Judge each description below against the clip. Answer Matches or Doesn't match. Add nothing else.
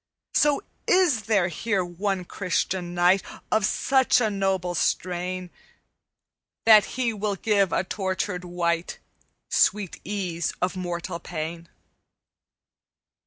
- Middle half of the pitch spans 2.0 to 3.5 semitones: Matches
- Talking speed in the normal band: Doesn't match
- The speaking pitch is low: Doesn't match